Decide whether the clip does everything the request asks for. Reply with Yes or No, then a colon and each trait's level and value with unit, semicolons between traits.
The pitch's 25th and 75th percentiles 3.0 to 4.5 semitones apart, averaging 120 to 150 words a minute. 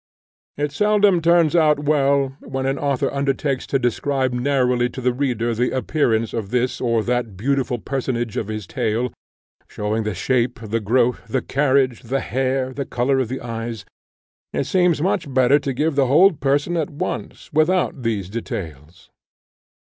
No: average, 3.4 semitones; average, 165 wpm